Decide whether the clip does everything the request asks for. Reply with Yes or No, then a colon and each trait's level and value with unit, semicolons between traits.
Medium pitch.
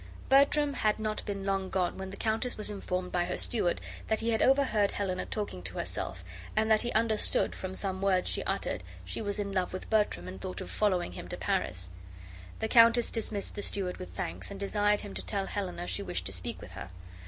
No: high, 200 Hz